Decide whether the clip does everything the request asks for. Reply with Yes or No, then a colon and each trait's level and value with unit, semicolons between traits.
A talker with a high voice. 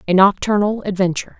Yes: high, 195 Hz